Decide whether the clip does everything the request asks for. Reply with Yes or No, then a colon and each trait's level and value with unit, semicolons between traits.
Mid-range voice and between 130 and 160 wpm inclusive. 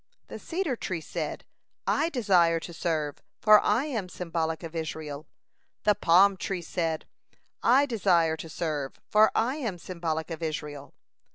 Yes: medium, 170 Hz; average, 150 wpm